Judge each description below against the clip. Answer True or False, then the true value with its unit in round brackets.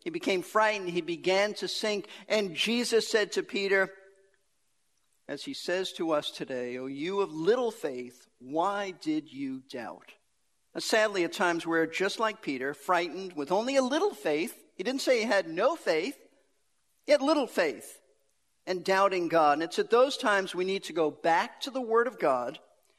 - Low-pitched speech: False (195 Hz)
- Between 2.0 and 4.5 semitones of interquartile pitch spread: False (5.4 semitones)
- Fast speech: False (180 wpm)